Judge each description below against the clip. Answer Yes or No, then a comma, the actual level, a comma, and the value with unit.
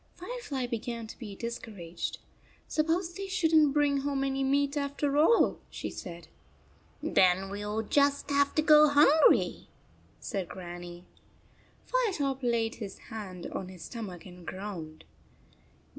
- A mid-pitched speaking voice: No, very high, 255 Hz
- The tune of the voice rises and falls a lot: Yes, wide, 7.2 semitones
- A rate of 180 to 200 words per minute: No, average, 145 wpm